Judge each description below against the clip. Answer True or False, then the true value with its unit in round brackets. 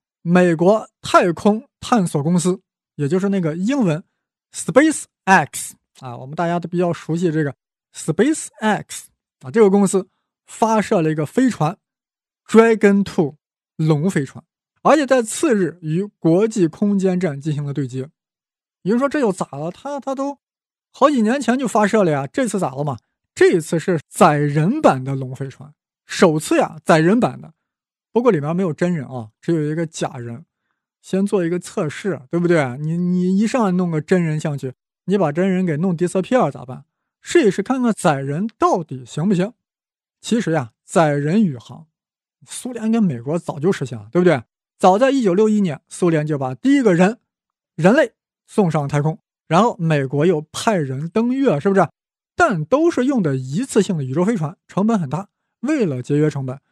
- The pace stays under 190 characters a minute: False (270 characters per minute)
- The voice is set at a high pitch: False (180 Hz)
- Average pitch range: False (5.7 semitones)